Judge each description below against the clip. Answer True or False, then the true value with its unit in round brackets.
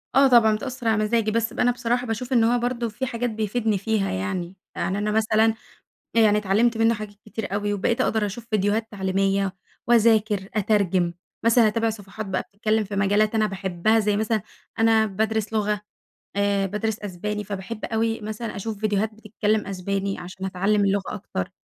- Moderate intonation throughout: False (2.2 semitones)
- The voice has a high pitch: True (215 Hz)